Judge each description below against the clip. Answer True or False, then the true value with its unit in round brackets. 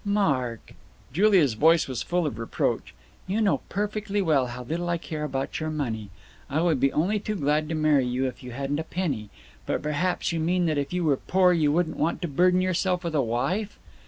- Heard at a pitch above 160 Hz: False (155 Hz)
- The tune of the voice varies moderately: True (4.7 semitones)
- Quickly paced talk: True (215 wpm)